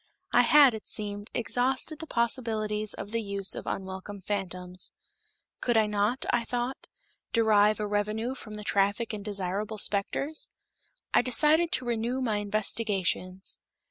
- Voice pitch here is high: Yes, high, 215 Hz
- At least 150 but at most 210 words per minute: No, average, 140 wpm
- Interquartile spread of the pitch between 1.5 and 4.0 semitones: Yes, average, 2.9 semitones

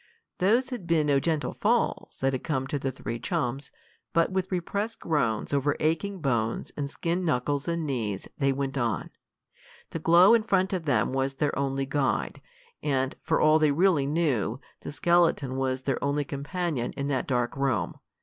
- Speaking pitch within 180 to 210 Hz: No, medium, 145 Hz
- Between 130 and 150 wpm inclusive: No, average, 180 wpm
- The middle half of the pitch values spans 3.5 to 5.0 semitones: Yes, average, 4.0 semitones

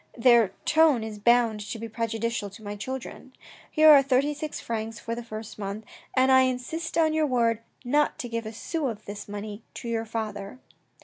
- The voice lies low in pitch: No, high, 230 Hz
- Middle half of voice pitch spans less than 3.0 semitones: No, average, 3.3 semitones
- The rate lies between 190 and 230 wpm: Yes, average, 195 wpm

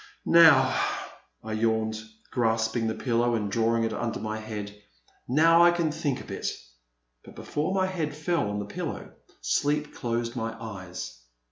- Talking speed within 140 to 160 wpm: Yes, average, 155 wpm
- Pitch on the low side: Yes, low, 115 Hz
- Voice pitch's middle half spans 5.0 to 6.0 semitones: Yes, wide, 5.5 semitones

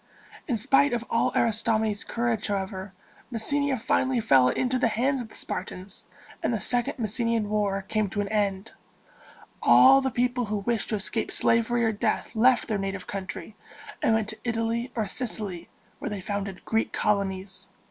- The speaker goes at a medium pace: Yes, average, 170 wpm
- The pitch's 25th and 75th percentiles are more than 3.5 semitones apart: No, average, 3.0 semitones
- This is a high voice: Yes, high, 220 Hz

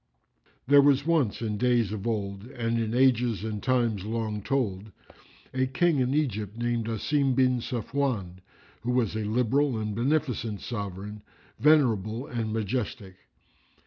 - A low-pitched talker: Yes, low, 115 Hz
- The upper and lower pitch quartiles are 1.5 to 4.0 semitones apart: Yes, average, 3.5 semitones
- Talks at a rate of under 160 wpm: Yes, average, 140 wpm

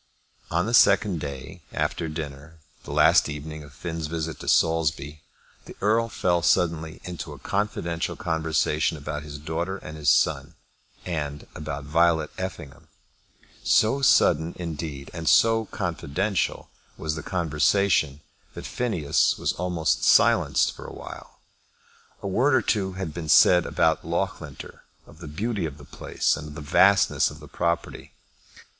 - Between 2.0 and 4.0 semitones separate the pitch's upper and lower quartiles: Yes, average, 3.2 semitones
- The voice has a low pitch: Yes, very low, 80 Hz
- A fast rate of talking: No, average, 145 wpm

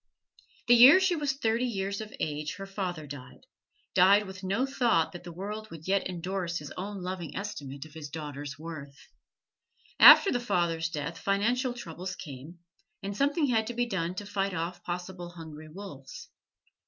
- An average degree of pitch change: Yes, average, 4.6 semitones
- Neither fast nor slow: Yes, average, 170 wpm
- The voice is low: No, medium, 185 Hz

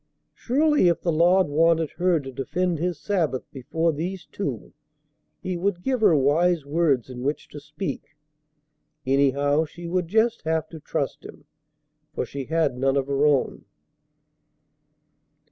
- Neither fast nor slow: Yes, average, 145 wpm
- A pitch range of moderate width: Yes, average, 4.0 semitones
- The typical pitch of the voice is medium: Yes, medium, 160 Hz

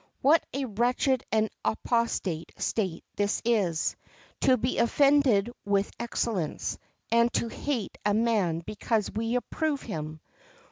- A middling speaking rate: No, slow, 120 wpm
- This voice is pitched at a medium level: No, high, 225 Hz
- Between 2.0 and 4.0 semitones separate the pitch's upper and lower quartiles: Yes, average, 3.7 semitones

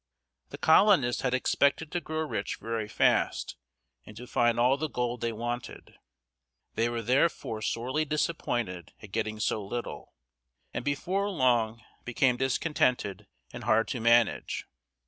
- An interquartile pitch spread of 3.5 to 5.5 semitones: Yes, average, 3.8 semitones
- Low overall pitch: Yes, low, 120 Hz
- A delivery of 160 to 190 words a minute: No, average, 140 wpm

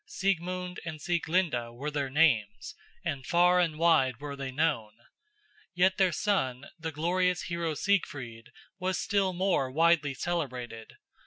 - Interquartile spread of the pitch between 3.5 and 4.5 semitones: No, average, 5.2 semitones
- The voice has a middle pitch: Yes, medium, 160 Hz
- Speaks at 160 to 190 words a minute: No, slow, 135 wpm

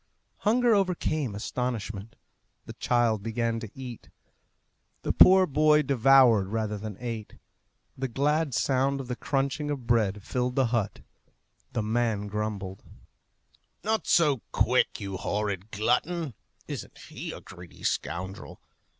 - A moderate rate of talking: No, slow, 125 wpm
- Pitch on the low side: Yes, low, 120 Hz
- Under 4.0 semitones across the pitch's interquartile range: No, average, 4.6 semitones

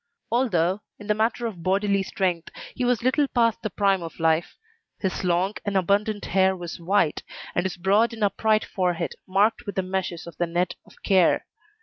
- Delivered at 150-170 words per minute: No, average, 190 wpm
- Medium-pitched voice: No, high, 195 Hz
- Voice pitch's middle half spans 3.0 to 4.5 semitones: Yes, average, 3.3 semitones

